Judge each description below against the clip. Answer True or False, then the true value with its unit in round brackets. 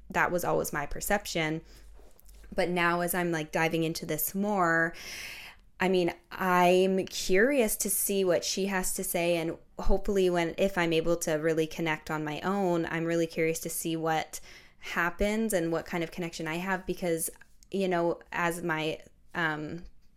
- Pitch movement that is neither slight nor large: False (2.2 semitones)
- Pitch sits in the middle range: True (175 Hz)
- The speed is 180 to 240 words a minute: False (170 wpm)